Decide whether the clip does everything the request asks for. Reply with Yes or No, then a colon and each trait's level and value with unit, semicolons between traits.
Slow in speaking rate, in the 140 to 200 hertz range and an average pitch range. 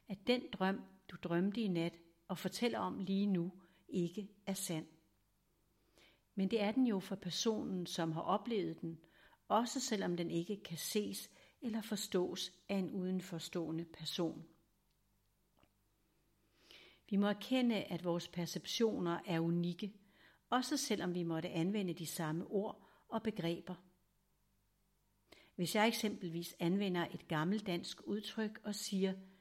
Yes: slow, 135 wpm; medium, 185 Hz; average, 3.5 semitones